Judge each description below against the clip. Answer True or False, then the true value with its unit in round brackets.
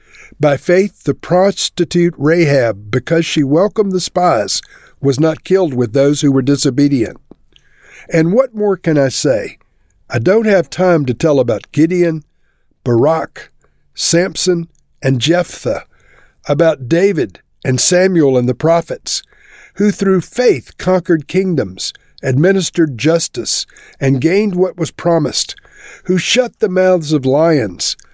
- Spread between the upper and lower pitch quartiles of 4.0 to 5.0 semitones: True (4.5 semitones)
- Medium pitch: True (170 Hz)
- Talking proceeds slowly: True (130 wpm)